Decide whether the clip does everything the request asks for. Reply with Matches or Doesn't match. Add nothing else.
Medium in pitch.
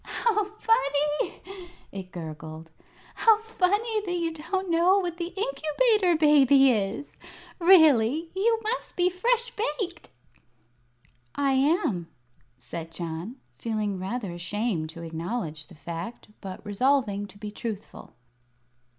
Doesn't match